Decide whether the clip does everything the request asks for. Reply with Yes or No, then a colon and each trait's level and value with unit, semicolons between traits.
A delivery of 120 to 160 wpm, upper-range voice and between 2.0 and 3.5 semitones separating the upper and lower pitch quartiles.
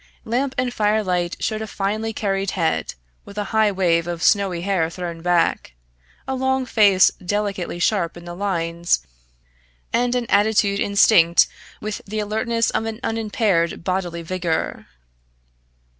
No: average, 145 wpm; high, 200 Hz; average, 3.9 semitones